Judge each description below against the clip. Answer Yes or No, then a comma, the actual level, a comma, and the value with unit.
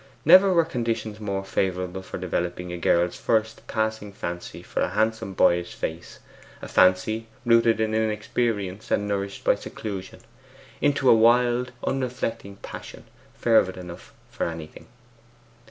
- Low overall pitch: Yes, low, 105 Hz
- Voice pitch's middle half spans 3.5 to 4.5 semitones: Yes, average, 3.9 semitones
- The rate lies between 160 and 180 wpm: No, slow, 135 wpm